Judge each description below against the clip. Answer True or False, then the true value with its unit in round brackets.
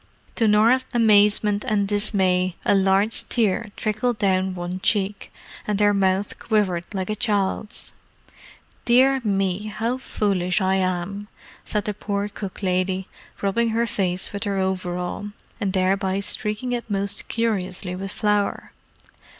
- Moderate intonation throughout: False (2.1 semitones)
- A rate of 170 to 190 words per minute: False (135 wpm)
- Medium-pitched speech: False (200 Hz)